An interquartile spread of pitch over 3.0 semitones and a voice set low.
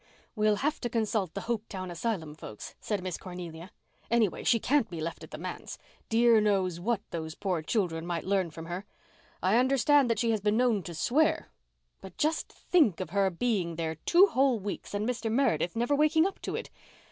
No: wide, 5.4 semitones; high, 210 Hz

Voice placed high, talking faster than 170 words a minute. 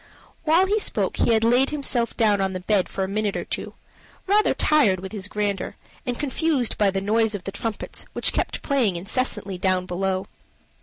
Yes: high, 210 Hz; average, 195 wpm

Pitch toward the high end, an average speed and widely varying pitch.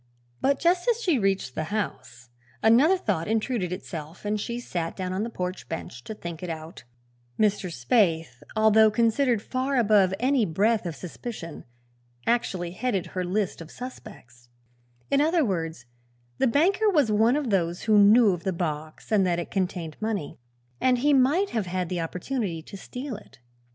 Yes: high, 205 Hz; average, 170 wpm; wide, 6.0 semitones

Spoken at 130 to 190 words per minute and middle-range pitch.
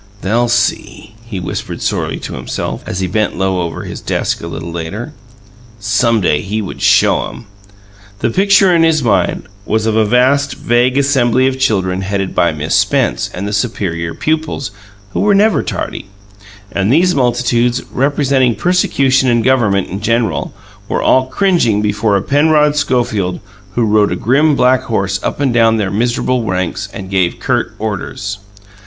No: average, 165 wpm; low, 115 Hz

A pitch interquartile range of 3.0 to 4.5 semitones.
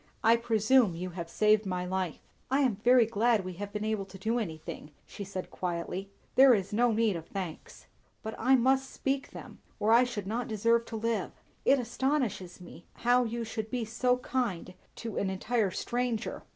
Yes: average, 4.1 semitones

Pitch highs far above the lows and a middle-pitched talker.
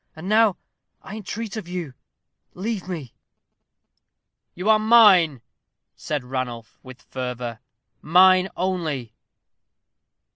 Yes: wide, 7.6 semitones; medium, 175 Hz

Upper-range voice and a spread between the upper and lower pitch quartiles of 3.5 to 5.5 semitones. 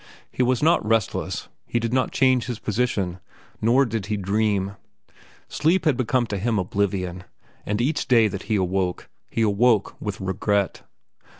No: low, 110 Hz; average, 3.9 semitones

